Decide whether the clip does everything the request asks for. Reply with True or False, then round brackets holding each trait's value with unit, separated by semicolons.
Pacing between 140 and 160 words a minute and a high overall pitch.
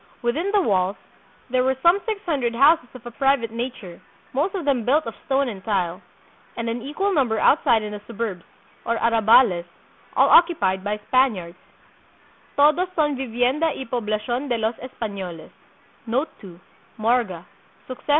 True (145 wpm; 240 Hz)